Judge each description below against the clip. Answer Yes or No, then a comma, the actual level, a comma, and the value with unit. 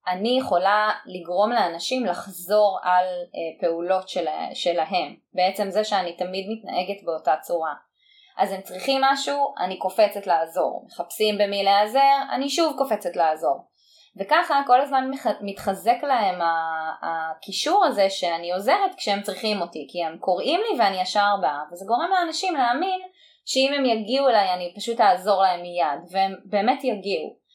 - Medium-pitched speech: No, high, 200 Hz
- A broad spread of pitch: Yes, wide, 6.7 semitones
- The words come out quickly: No, average, 140 wpm